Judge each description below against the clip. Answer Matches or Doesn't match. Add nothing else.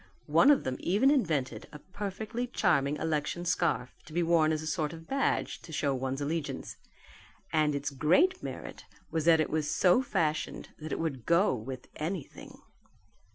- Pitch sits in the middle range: Matches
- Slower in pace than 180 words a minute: Matches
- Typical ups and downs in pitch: Matches